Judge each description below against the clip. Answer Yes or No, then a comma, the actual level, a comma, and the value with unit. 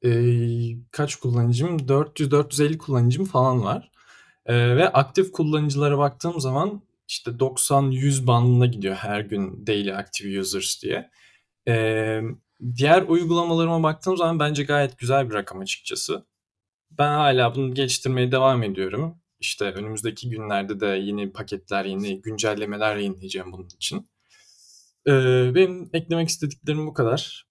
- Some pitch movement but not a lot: No, wide, 5.8 semitones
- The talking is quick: No, average, 125 wpm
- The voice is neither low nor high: No, low, 125 Hz